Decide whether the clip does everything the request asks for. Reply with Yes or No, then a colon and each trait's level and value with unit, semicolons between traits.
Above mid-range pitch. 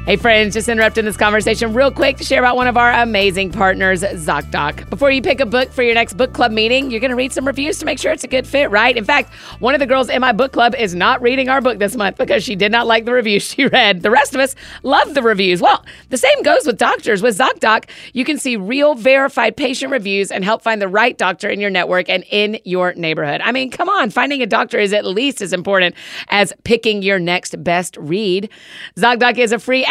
Yes: high, 235 Hz